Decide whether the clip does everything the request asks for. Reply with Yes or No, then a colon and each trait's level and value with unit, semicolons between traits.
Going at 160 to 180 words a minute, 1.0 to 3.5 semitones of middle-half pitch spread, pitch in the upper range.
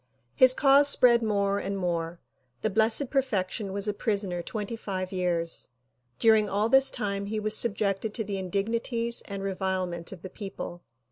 Yes: average, 165 wpm; average, 3.1 semitones; high, 200 Hz